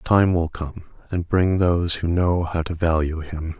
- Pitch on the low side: Yes, very low, 85 Hz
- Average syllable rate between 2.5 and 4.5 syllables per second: Yes, 4.3 syllables/s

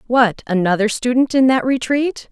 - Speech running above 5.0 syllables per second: No, 4.8 syllables/s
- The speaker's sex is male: No, female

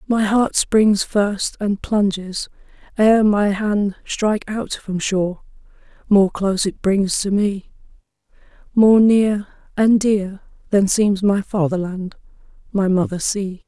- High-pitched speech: Yes, high, 200 Hz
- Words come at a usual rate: No, slow, 130 wpm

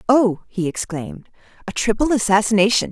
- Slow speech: Yes, slow, 125 wpm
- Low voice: No, high, 215 Hz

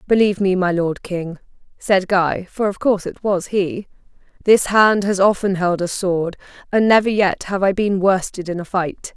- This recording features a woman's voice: Yes, female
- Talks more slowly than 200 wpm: Yes, average, 190 wpm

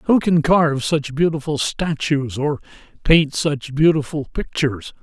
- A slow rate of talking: Yes, slow, 130 wpm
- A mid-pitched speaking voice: Yes, medium, 150 Hz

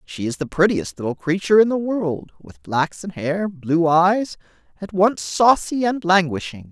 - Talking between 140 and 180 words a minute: Yes, average, 160 wpm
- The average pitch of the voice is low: No, medium, 175 Hz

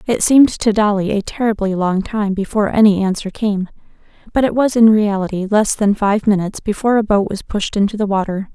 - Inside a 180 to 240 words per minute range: Yes, fast, 205 wpm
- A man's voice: No, female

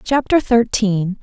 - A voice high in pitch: Yes, high, 225 Hz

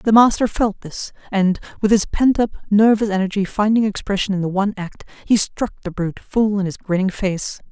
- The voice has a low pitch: No, high, 200 Hz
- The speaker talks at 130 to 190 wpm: No, average, 200 wpm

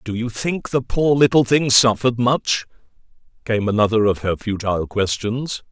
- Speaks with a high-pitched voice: No, low, 115 Hz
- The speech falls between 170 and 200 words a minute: No, average, 160 wpm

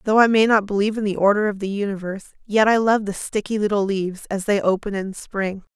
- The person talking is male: No, female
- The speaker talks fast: Yes, fast, 240 wpm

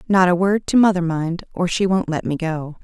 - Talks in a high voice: No, medium, 175 Hz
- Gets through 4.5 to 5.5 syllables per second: Yes, 5.1 syllables/s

